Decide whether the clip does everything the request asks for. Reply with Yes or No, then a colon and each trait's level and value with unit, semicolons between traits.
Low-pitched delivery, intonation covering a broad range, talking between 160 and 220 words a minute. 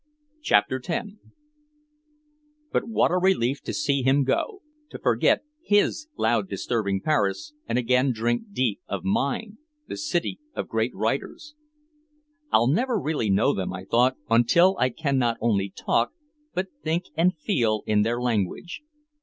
No: low, 130 Hz; wide, 7.7 semitones; average, 145 wpm